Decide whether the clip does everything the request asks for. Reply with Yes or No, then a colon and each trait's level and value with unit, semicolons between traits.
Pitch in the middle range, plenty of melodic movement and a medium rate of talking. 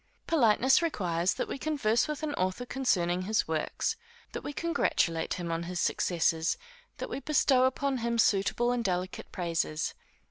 No: high, 215 Hz; wide, 7.3 semitones; average, 155 wpm